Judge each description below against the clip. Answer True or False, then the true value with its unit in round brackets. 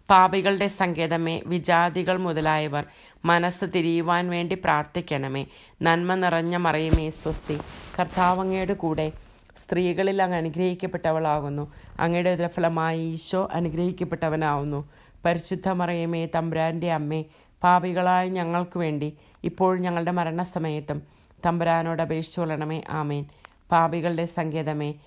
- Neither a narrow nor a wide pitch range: False (2.2 semitones)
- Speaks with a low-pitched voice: False (170 Hz)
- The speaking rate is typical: False (85 wpm)